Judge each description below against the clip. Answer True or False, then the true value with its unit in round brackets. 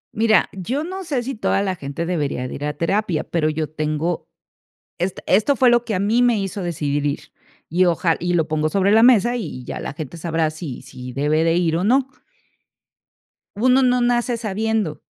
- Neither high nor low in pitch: True (180 Hz)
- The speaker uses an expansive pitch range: True (6.7 semitones)